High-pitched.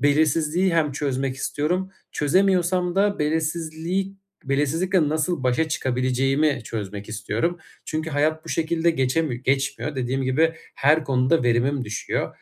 No: medium, 150 Hz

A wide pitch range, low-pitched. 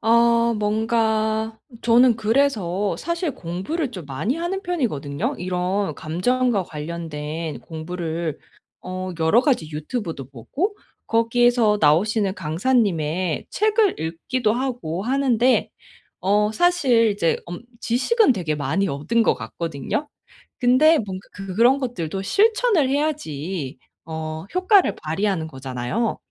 No: wide, 7.3 semitones; high, 210 Hz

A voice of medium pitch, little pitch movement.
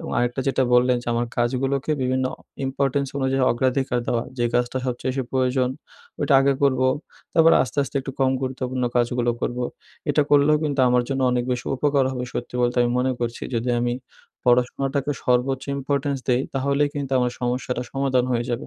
No: low, 130 Hz; narrow, 1.8 semitones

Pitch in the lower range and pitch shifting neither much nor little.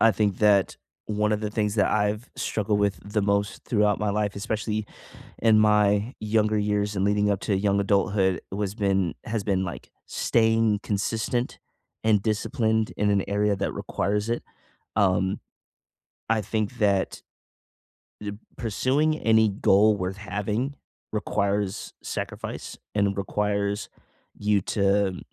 No: low, 105 Hz; narrow, 1.3 semitones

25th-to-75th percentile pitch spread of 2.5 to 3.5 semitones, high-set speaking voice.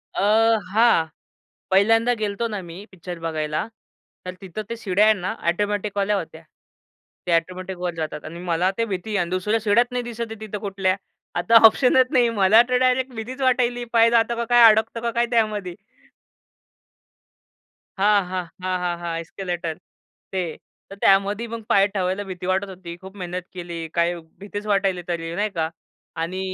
No: average, 4.0 semitones; high, 195 Hz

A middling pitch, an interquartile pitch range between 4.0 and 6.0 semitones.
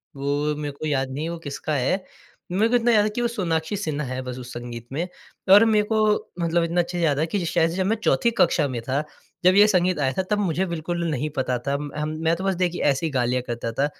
Yes: medium, 160 Hz; average, 4.9 semitones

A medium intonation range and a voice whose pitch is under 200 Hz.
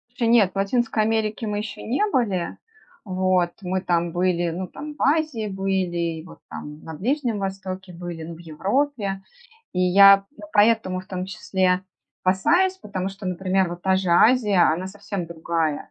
Yes: average, 3.2 semitones; high, 190 Hz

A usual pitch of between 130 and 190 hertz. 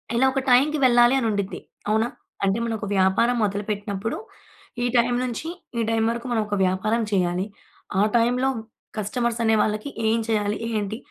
No: high, 225 Hz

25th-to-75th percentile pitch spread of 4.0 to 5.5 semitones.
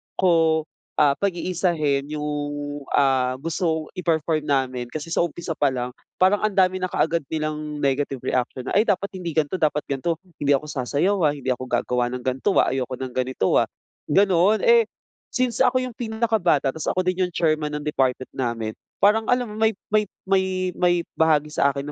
Yes: average, 5.1 semitones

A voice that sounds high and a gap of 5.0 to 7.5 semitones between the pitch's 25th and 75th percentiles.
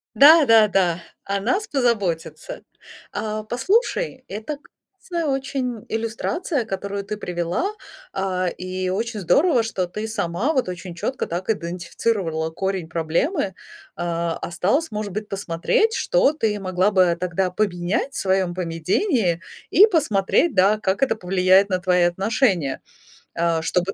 Yes: high, 195 Hz; wide, 5.4 semitones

